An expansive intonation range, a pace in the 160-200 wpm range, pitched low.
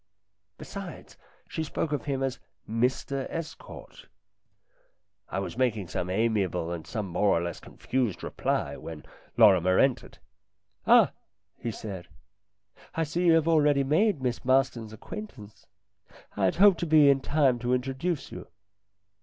Yes: wide, 6.5 semitones; average, 170 wpm; low, 125 Hz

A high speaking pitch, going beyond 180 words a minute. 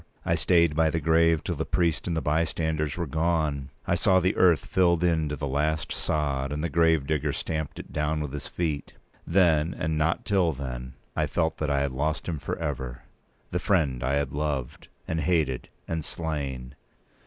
No: very low, 80 Hz; average, 190 wpm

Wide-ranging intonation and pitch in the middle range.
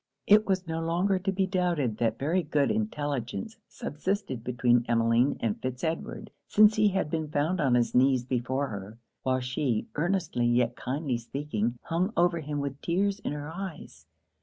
Yes: wide, 6.6 semitones; medium, 145 Hz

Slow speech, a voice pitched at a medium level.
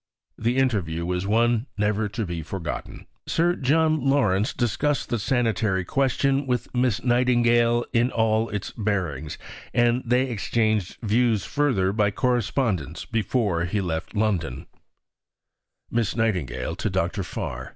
No: slow, 130 wpm; low, 115 Hz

